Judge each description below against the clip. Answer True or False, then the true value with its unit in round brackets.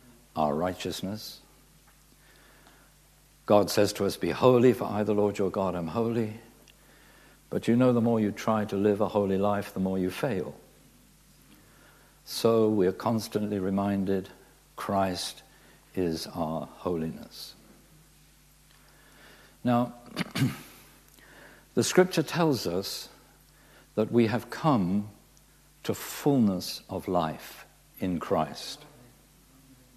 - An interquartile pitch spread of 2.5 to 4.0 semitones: True (3.4 semitones)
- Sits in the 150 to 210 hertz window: False (105 Hz)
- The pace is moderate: False (110 wpm)